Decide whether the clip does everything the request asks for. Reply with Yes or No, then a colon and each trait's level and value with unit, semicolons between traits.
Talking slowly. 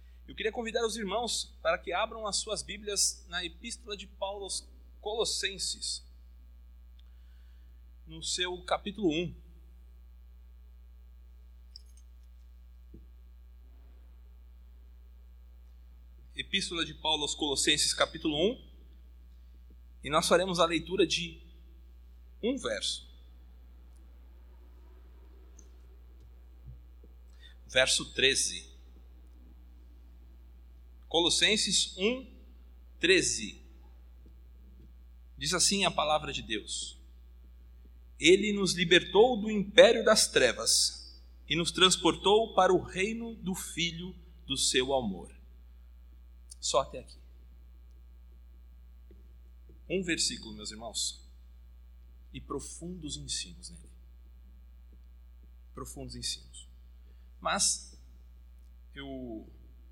Yes: slow, 80 wpm